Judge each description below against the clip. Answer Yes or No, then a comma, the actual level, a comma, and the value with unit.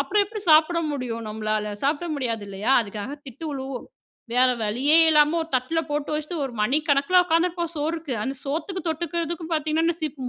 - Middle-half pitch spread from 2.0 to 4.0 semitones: No, average, 4.5 semitones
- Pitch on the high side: Yes, very high, 295 Hz